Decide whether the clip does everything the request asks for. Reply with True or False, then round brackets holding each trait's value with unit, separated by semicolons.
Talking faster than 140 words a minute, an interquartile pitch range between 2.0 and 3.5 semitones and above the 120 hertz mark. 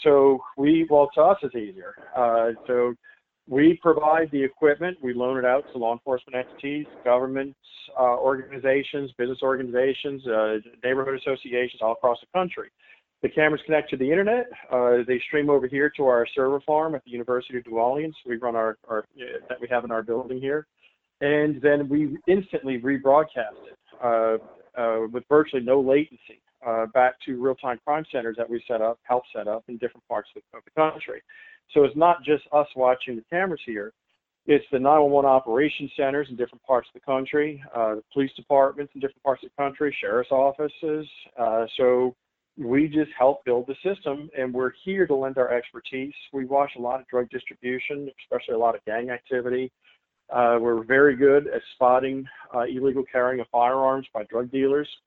True (190 wpm; 3.0 semitones; 135 Hz)